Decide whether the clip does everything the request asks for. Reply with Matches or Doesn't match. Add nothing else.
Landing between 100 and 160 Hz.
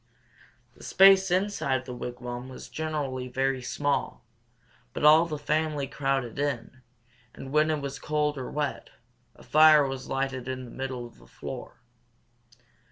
Matches